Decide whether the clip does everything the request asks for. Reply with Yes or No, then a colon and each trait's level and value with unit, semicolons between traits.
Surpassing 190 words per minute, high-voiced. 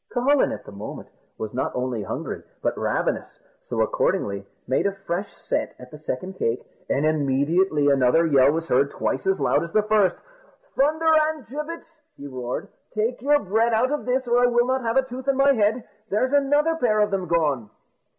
Yes: average, 200 wpm; high, 205 Hz